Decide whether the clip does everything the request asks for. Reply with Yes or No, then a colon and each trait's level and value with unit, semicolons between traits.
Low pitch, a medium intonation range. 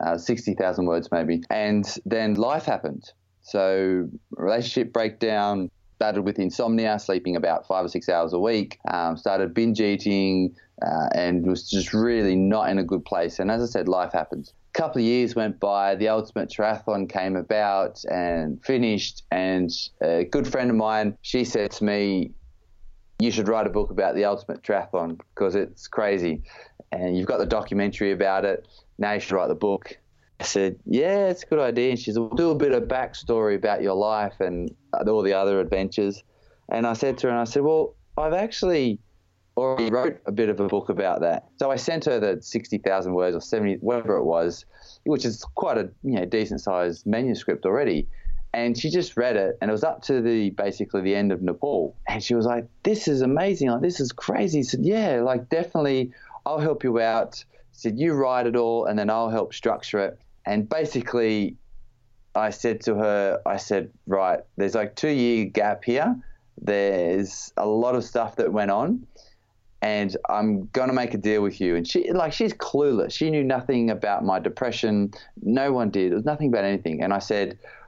Yes: low, 110 Hz; average, 3.8 semitones